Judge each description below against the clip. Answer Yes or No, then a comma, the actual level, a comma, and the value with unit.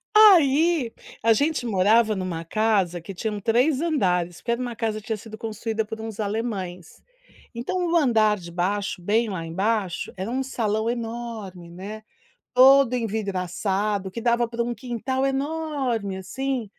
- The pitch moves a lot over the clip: No, average, 4.0 semitones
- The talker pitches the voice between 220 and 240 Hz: Yes, high, 225 Hz